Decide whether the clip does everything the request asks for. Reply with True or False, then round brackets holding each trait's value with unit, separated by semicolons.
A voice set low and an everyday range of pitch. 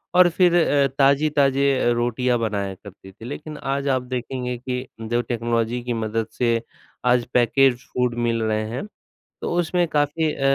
True (125 Hz; 3.1 semitones)